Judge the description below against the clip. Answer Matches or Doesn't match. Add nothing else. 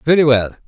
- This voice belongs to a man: Matches